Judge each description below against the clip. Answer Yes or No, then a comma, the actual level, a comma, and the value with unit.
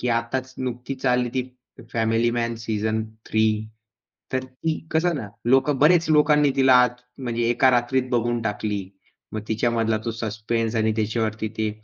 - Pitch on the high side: No, low, 120 Hz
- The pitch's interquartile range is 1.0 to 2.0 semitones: No, average, 2.7 semitones